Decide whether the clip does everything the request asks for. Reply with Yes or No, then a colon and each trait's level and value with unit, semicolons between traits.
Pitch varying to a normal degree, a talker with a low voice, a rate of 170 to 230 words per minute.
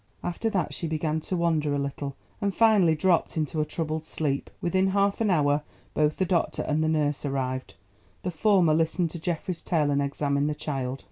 No: average, 3.4 semitones; medium, 155 Hz; average, 195 wpm